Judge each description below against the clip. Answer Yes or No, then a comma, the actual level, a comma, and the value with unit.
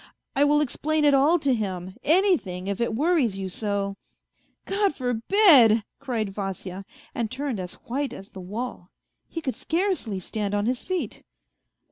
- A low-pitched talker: No, high, 235 Hz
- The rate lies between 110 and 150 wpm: No, average, 170 wpm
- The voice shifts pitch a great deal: Yes, wide, 7.0 semitones